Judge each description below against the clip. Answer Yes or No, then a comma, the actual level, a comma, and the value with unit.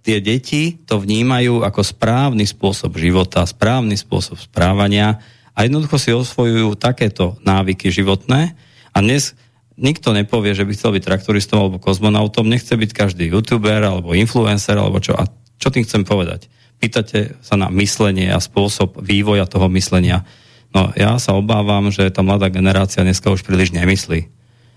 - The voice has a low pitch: Yes, low, 105 Hz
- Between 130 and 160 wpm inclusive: Yes, average, 155 wpm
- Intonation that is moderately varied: Yes, average, 3.5 semitones